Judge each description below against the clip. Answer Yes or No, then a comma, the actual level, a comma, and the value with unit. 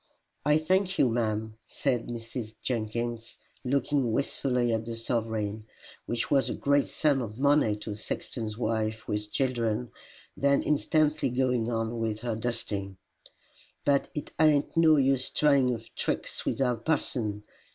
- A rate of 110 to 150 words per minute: Yes, average, 145 wpm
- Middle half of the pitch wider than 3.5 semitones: Yes, average, 4.0 semitones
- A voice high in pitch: No, low, 120 Hz